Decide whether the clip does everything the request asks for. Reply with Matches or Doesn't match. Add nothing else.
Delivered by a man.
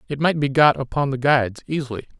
Matches